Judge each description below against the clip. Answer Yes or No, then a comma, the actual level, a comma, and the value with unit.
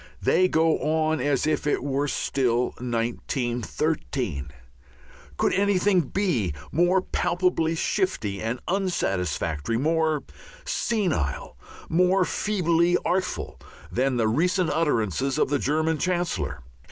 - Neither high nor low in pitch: Yes, medium, 155 Hz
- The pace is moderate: No, slow, 105 wpm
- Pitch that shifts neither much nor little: No, wide, 6.8 semitones